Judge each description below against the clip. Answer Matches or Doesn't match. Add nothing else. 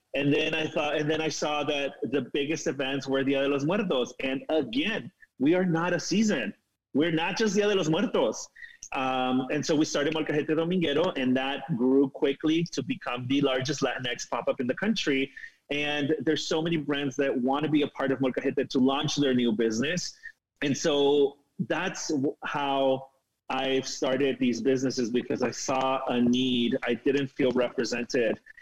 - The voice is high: Doesn't match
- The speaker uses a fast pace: Doesn't match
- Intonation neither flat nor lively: Matches